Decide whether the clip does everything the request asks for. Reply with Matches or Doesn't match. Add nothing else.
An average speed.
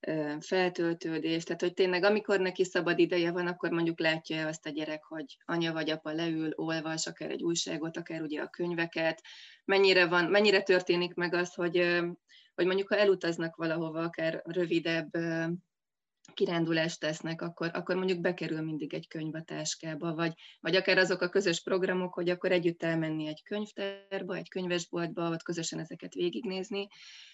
Doesn't match